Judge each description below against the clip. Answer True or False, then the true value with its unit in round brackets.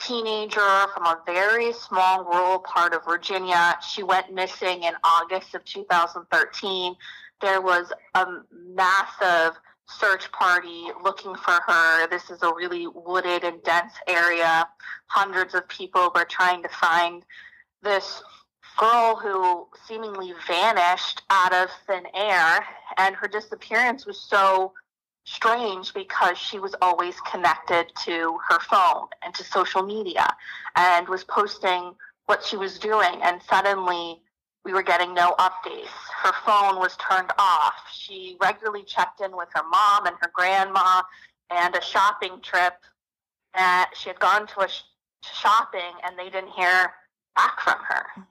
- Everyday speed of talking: True (145 wpm)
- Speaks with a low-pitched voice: False (185 Hz)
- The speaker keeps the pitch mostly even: True (2.1 semitones)